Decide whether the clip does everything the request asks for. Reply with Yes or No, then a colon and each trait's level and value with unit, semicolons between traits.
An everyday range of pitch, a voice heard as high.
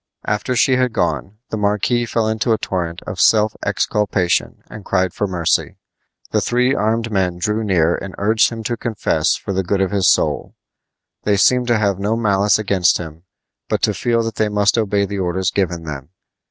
No: average, 3.1 semitones; low, 105 Hz